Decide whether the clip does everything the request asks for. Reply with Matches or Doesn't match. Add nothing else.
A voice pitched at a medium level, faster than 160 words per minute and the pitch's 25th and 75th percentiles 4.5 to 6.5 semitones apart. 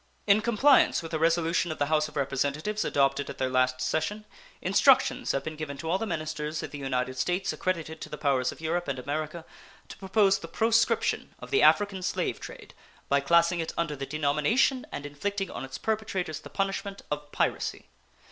Matches